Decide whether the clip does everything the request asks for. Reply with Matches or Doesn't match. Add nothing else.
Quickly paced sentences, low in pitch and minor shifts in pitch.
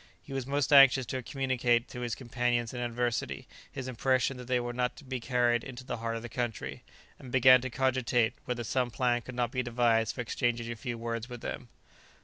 Matches